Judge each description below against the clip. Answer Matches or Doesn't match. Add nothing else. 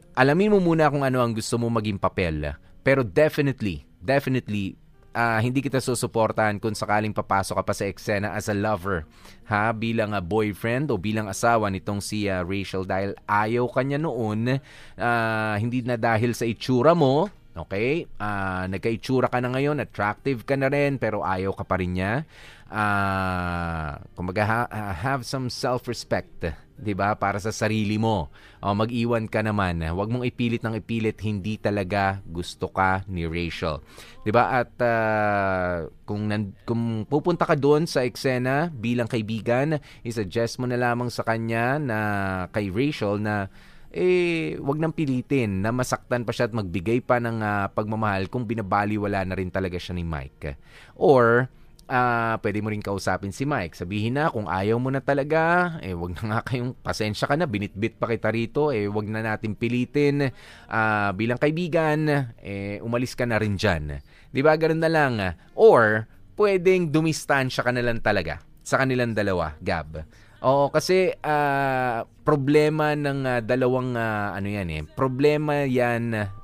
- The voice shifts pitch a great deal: Doesn't match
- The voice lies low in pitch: Matches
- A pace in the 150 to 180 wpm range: Matches